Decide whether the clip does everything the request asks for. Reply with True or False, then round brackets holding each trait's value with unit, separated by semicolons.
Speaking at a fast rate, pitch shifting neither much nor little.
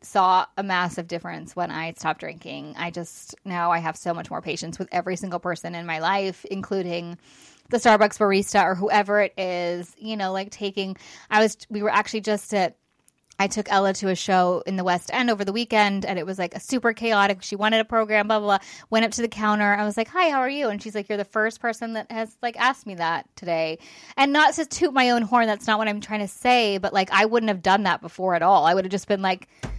True (255 wpm; 3.3 semitones)